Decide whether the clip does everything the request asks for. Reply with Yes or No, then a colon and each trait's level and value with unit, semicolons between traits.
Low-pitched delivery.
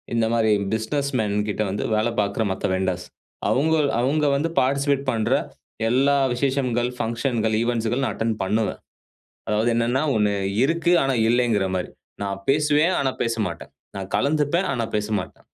Yes: low, 120 Hz